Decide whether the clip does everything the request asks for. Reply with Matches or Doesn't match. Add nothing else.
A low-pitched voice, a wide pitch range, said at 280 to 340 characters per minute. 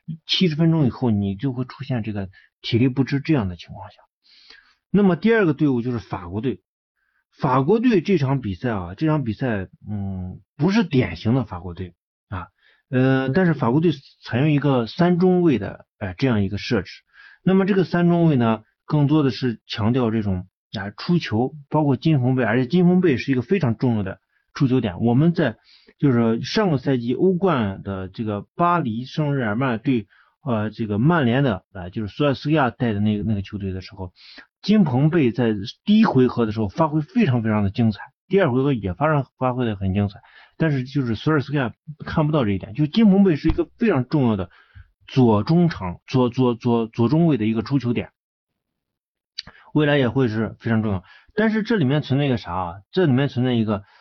Matches